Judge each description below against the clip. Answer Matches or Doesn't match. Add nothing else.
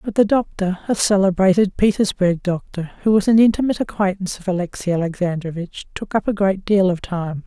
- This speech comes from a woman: Matches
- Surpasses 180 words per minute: Doesn't match